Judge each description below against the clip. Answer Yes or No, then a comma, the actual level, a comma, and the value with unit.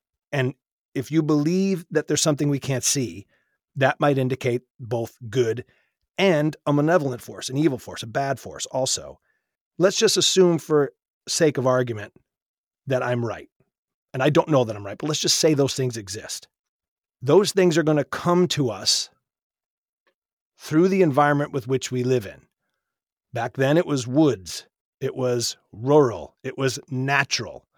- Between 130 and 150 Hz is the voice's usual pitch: Yes, low, 135 Hz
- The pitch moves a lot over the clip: No, average, 3.6 semitones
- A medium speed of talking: Yes, average, 165 wpm